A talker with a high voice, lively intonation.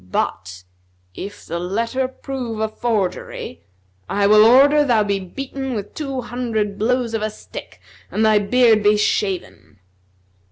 No: high, 220 Hz; average, 3.7 semitones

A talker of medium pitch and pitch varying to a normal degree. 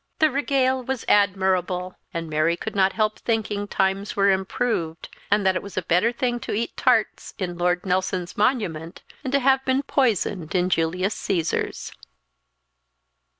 No: high, 195 Hz; average, 4.7 semitones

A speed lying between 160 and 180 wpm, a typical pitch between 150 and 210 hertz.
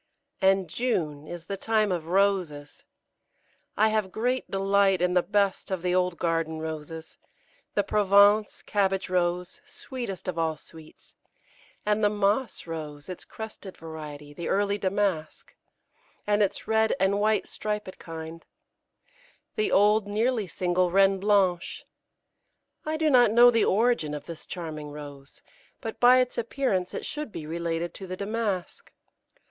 No: average, 145 wpm; high, 190 Hz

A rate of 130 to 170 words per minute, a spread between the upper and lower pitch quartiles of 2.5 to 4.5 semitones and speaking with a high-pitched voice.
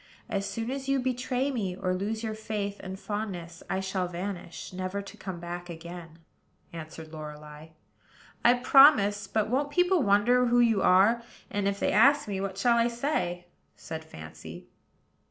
No: average, 165 wpm; average, 5.1 semitones; high, 200 Hz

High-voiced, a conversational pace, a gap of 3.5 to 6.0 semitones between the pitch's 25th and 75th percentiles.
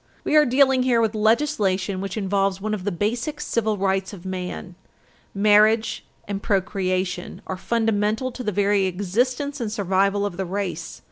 No: high, 205 Hz; average, 160 wpm; average, 3.1 semitones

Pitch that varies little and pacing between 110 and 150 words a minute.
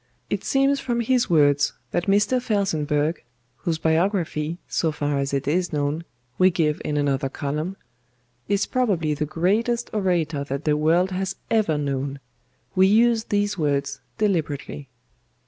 No: wide, 5.6 semitones; average, 145 wpm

